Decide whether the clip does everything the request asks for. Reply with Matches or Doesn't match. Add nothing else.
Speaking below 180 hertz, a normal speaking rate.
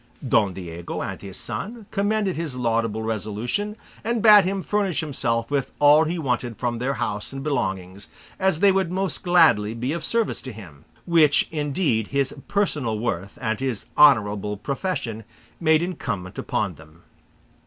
Matches